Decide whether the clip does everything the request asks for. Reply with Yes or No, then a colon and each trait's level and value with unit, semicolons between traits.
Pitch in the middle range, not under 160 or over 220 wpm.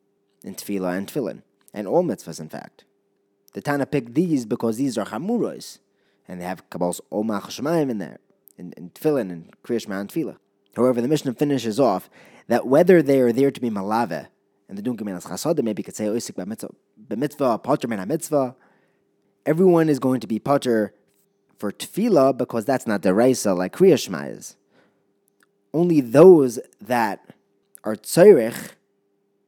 No: low, 110 Hz; average, 165 wpm